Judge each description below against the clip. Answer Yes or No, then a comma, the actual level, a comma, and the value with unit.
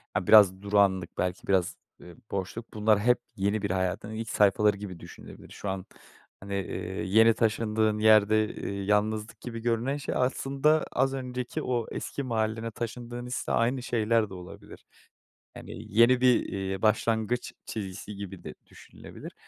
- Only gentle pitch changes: No, average, 3.0 semitones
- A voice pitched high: No, low, 110 Hz